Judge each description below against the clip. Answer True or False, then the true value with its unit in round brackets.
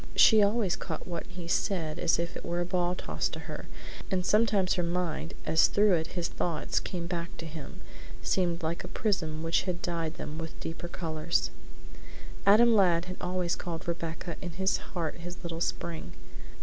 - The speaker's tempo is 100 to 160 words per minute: False (180 wpm)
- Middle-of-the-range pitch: True (175 Hz)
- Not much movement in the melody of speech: True (1.9 semitones)